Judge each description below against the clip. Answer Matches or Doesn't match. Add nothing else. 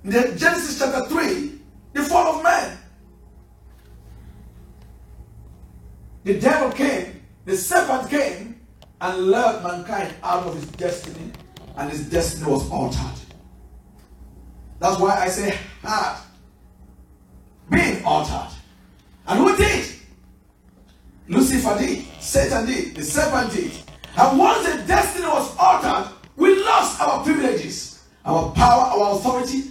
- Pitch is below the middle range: Doesn't match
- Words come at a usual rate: Doesn't match